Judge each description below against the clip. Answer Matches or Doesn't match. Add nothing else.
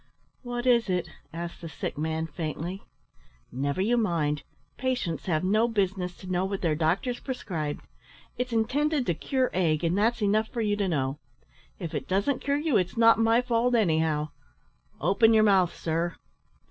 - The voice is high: Matches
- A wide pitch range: Matches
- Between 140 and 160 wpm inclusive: Doesn't match